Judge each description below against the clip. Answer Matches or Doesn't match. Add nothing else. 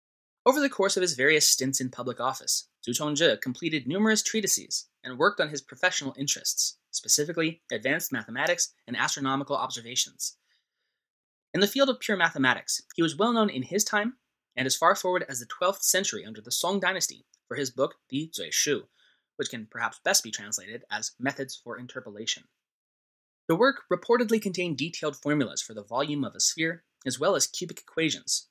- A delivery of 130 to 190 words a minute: Matches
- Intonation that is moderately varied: Doesn't match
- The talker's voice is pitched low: Doesn't match